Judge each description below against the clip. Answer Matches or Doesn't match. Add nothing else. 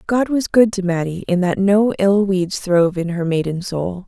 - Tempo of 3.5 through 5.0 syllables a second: Matches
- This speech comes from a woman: Matches